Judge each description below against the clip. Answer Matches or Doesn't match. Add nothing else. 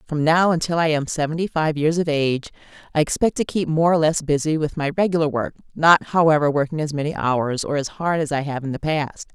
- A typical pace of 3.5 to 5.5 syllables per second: Doesn't match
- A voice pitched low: Doesn't match